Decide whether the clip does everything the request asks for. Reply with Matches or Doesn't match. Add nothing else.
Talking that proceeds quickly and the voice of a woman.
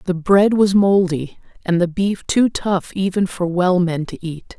Doesn't match